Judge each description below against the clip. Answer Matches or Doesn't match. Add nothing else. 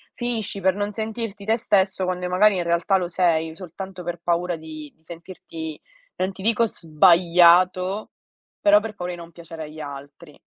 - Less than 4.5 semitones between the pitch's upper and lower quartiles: Matches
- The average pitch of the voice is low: Doesn't match